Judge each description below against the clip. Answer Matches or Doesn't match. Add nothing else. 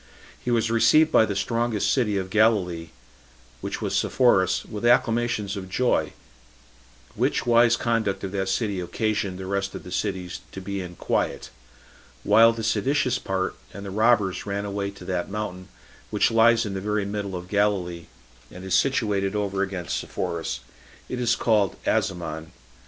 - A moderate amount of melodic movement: Matches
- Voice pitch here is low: Matches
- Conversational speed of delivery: Matches